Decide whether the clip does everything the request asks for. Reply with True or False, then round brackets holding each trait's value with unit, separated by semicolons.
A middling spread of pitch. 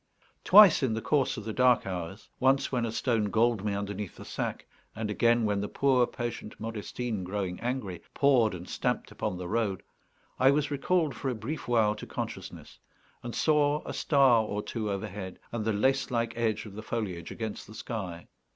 True (3.8 semitones)